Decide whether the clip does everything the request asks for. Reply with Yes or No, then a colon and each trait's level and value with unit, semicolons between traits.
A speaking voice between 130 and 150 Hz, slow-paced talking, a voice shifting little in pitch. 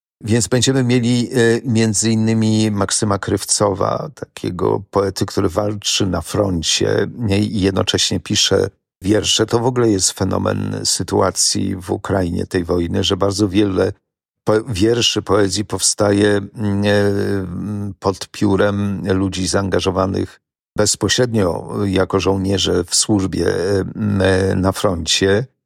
No: low, 100 Hz; slow, 105 wpm; narrow, 2.1 semitones